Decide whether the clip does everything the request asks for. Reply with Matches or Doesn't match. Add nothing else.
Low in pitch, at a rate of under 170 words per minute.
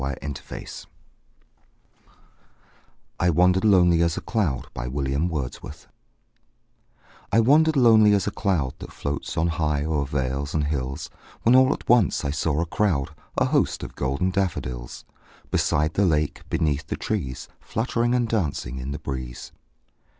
Matches